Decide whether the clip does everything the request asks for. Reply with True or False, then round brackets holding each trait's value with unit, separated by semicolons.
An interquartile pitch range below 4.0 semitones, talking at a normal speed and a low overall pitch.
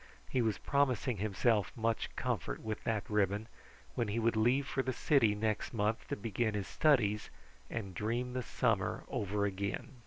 True (2.8 semitones; 165 wpm; 110 Hz)